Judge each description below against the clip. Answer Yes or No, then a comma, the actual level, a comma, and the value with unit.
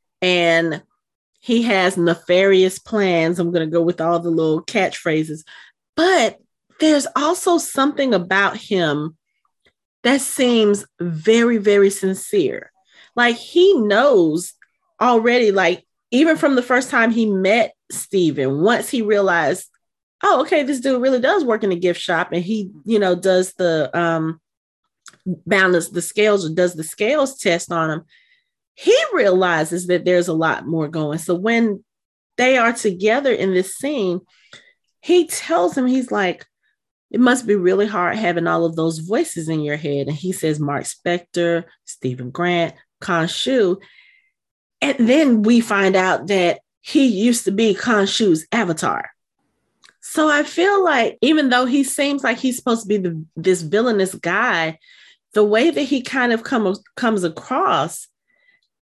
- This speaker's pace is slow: No, average, 155 wpm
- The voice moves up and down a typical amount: No, wide, 6.5 semitones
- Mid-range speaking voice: No, high, 200 Hz